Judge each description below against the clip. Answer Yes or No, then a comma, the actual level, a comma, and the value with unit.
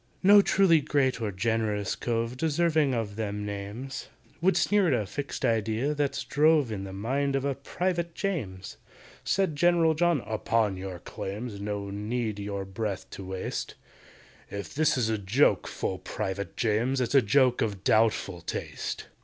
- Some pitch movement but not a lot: No, wide, 6.1 semitones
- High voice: No, low, 115 Hz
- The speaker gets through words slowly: No, average, 160 wpm